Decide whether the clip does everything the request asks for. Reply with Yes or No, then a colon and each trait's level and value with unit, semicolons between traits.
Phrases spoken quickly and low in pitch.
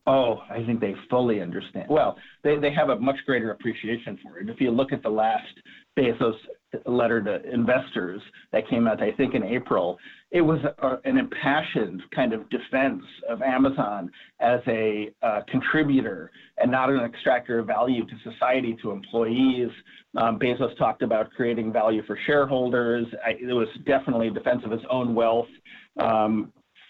No: average, 170 wpm; low, 125 Hz